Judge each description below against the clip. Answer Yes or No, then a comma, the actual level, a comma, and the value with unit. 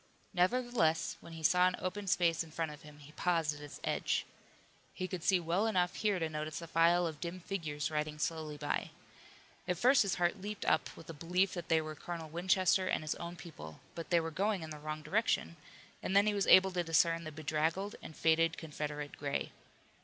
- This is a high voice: No, medium, 165 Hz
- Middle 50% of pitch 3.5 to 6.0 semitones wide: No, average, 3.0 semitones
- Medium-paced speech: No, fast, 215 wpm